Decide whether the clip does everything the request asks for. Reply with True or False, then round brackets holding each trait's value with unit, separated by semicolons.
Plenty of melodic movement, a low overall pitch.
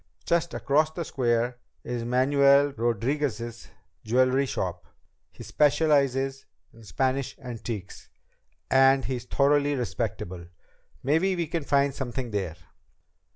False (3.2 semitones; 130 Hz)